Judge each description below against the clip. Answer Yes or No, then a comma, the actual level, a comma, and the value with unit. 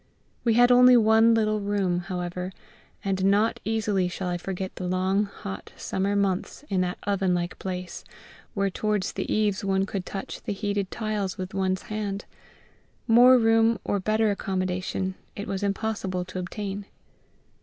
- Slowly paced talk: No, average, 155 wpm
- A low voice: No, high, 195 Hz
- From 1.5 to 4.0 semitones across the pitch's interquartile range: Yes, narrow, 2.4 semitones